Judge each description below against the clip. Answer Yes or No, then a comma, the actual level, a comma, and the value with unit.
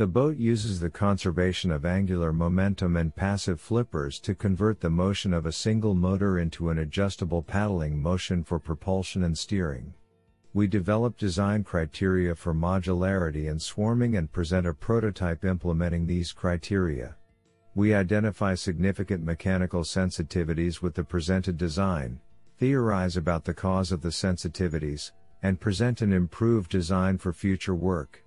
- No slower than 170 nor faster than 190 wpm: No, average, 140 wpm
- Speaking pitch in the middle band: No, very low, 95 Hz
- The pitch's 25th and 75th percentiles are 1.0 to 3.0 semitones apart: Yes, average, 2.7 semitones